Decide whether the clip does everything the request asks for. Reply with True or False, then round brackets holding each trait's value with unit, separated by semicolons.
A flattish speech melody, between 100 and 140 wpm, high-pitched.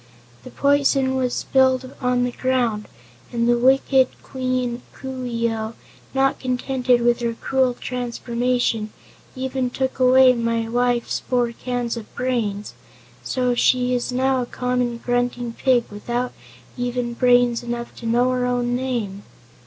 True (1.3 semitones; 135 wpm; 245 Hz)